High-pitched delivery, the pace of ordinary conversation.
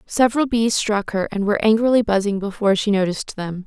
Yes: high, 210 Hz; average, 195 wpm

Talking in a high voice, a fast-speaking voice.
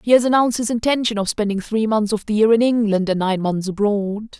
Yes: high, 215 Hz; fast, 245 wpm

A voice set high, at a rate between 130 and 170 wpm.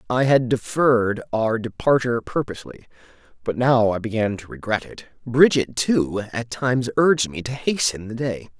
No: low, 120 Hz; average, 160 wpm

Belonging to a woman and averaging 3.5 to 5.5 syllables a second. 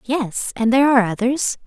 Yes: female; 5.4 syllables/s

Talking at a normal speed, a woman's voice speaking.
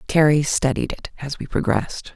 Yes: average, 165 wpm; female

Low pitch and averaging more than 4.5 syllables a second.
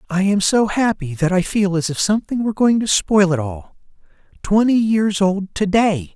No: high, 195 Hz; 4.9 syllables/s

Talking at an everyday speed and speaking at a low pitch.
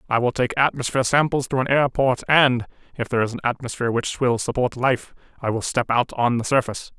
No: fast, 225 wpm; low, 125 Hz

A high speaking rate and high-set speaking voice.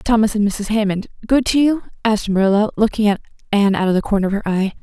Yes: fast, 225 wpm; high, 210 Hz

